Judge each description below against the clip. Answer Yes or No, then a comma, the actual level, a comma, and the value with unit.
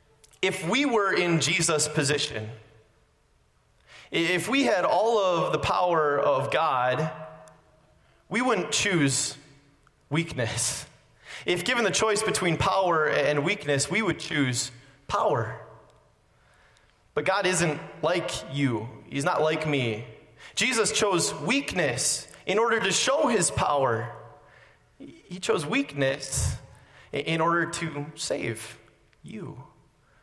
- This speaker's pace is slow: Yes, slow, 115 wpm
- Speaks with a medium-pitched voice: Yes, medium, 150 Hz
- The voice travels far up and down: No, average, 4.0 semitones